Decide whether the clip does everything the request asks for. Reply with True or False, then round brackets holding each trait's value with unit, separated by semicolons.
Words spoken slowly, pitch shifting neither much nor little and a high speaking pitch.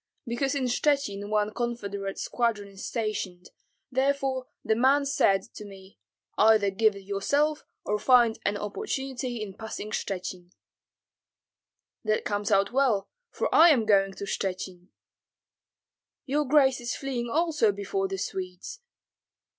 True (130 wpm; 4.9 semitones; 215 Hz)